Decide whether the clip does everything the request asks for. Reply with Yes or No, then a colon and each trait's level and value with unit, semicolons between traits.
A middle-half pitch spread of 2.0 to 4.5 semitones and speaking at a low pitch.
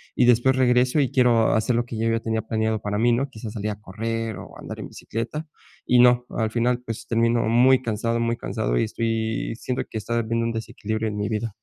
No: narrow, 1.6 semitones; low, 115 Hz